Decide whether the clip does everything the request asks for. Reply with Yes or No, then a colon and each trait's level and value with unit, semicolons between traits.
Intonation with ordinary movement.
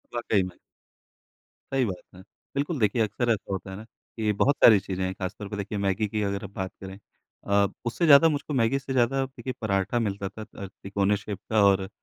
Yes: average, 3.5 semitones